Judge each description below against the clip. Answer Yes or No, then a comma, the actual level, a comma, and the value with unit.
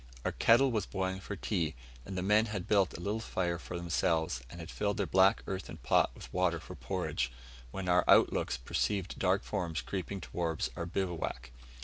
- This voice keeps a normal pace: Yes, average, 195 wpm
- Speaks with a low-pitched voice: Yes, very low, 90 Hz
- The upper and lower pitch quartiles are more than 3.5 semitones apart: No, average, 2.8 semitones